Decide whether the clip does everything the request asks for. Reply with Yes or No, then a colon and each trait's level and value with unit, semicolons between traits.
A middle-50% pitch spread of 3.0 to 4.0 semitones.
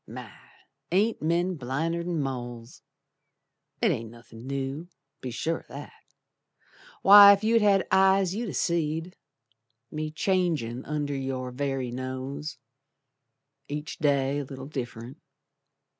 No: average, 5.1 semitones